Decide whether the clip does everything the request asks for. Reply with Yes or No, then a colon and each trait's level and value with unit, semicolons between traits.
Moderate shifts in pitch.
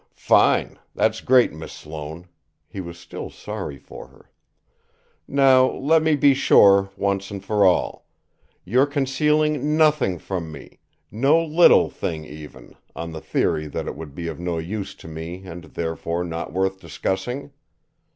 No: wide, 8.5 semitones